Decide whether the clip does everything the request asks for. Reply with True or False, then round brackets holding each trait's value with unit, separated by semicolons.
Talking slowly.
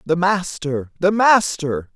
True (125 wpm)